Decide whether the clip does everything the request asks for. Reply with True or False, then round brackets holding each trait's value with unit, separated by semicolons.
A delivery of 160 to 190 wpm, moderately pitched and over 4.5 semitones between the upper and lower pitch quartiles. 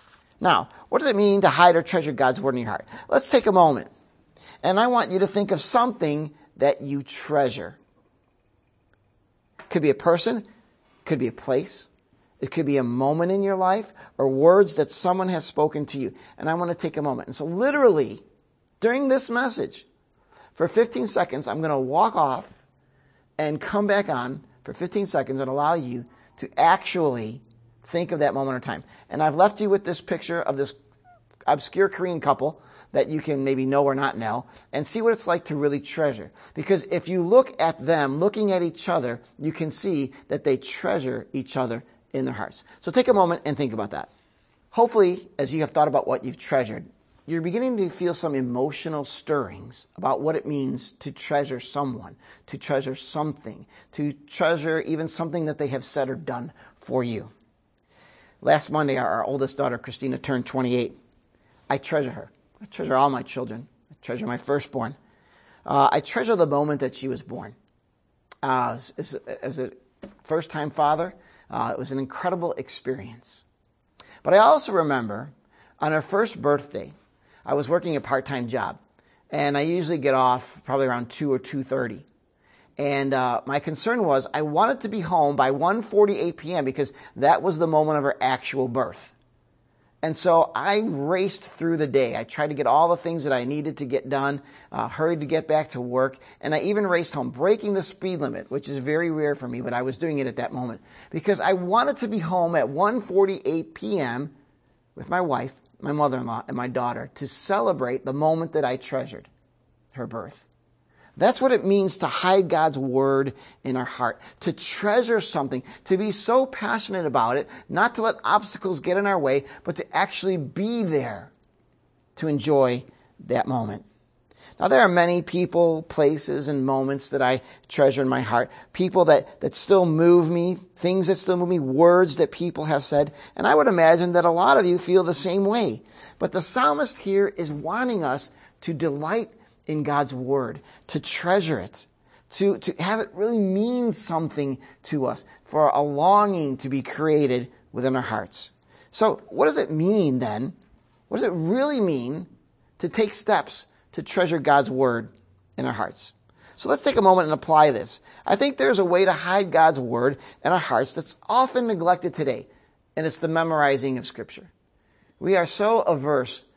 True (185 wpm; 150 Hz; 5.3 semitones)